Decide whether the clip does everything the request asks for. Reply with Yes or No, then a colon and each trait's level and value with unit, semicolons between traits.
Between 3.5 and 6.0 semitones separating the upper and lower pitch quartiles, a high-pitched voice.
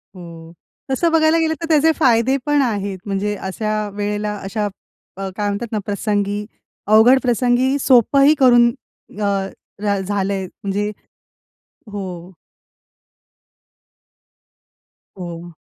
Yes: average, 4.3 semitones; high, 210 Hz